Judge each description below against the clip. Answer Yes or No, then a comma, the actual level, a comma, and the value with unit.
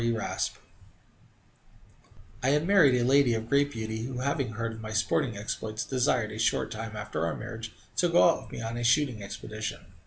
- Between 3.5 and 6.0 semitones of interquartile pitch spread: No, average, 3.1 semitones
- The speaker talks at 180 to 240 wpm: Yes, average, 195 wpm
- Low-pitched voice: Yes, low, 115 Hz